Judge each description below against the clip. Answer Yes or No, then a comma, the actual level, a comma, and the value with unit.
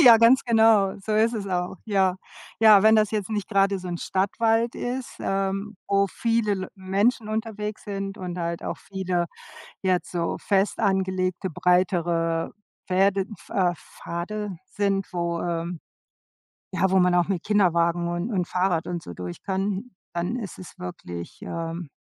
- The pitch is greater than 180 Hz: Yes, high, 190 Hz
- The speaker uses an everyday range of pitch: Yes, average, 3.0 semitones